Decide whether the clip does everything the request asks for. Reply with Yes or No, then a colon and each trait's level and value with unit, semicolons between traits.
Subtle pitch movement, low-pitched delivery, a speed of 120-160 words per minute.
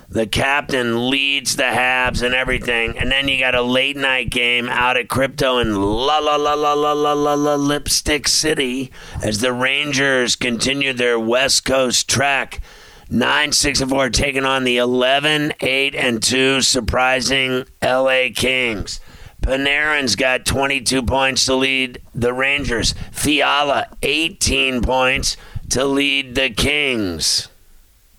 Yes: narrow, 2.0 semitones; low, 130 Hz; average, 145 wpm